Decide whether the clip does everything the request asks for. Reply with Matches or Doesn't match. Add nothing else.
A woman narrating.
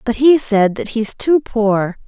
Matches